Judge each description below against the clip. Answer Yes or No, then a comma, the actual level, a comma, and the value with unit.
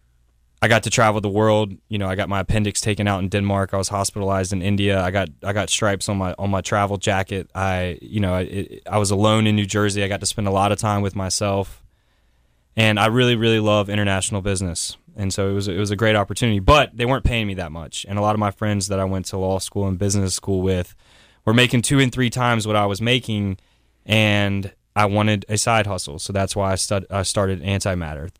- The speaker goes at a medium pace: No, fast, 245 wpm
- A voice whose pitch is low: Yes, low, 100 Hz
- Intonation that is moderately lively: No, narrow, 1.7 semitones